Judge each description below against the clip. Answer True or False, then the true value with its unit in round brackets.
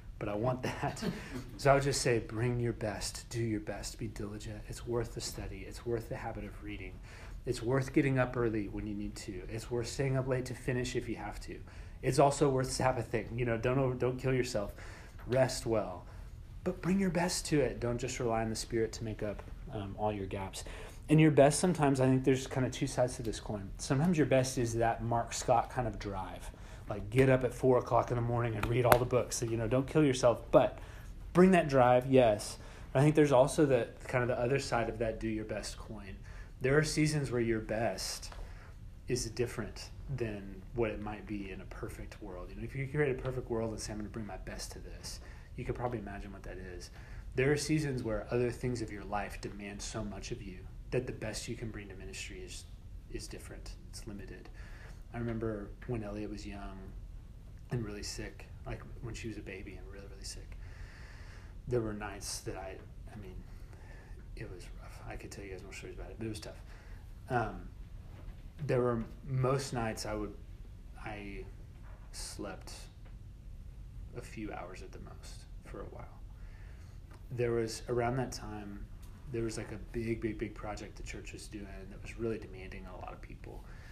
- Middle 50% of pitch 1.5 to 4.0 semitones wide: True (3.7 semitones)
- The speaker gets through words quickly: True (215 wpm)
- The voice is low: True (110 Hz)